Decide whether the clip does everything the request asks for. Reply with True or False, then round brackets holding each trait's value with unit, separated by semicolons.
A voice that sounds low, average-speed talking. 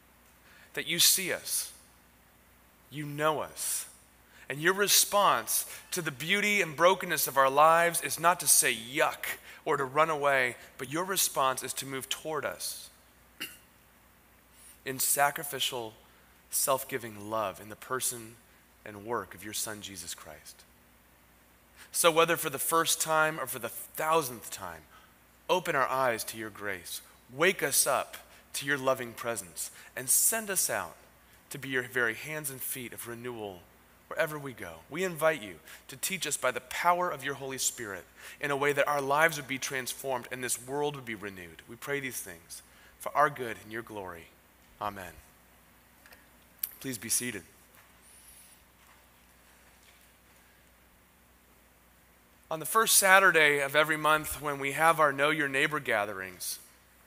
True (120 Hz; 155 wpm)